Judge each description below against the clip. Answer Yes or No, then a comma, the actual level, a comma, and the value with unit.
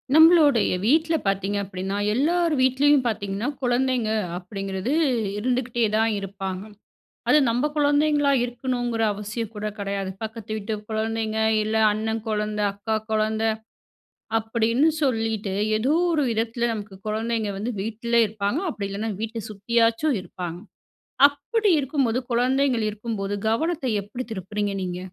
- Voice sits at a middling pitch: No, high, 225 Hz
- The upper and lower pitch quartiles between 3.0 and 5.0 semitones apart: Yes, average, 3.8 semitones